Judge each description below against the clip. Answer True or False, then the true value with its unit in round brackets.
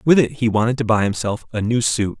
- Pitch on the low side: True (115 Hz)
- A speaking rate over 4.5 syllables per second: True (6.0 syllables/s)